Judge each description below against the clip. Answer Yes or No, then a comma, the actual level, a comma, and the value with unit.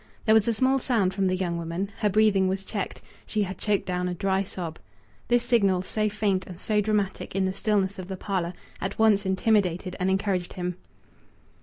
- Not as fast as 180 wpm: No, average, 200 wpm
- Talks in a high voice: Yes, high, 195 Hz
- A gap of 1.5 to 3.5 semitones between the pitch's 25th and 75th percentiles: Yes, narrow, 2.4 semitones